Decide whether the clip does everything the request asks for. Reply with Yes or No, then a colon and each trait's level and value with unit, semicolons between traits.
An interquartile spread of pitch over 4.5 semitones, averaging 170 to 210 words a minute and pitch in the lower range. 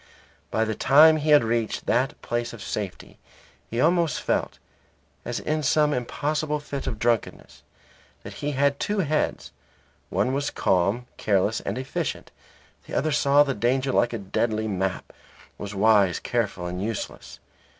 No: wide, 5.4 semitones; average, 150 wpm; low, 120 Hz